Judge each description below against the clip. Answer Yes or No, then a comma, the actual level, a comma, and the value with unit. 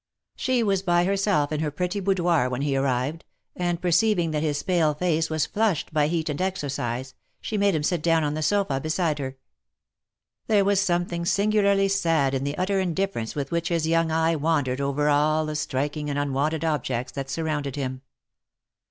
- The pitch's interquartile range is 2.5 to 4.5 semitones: Yes, average, 3.9 semitones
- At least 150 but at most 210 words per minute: Yes, average, 190 wpm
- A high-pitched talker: No, medium, 160 Hz